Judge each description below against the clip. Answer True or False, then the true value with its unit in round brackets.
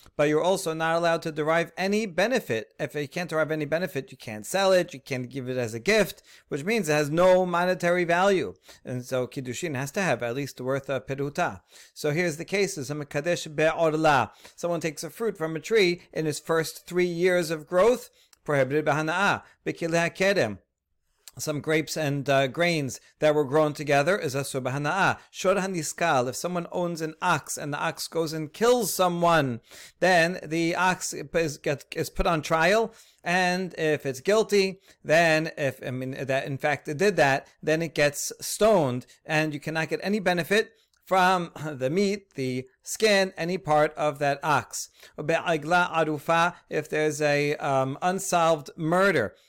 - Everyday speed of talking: True (165 wpm)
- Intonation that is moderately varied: True (3.8 semitones)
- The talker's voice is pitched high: False (160 Hz)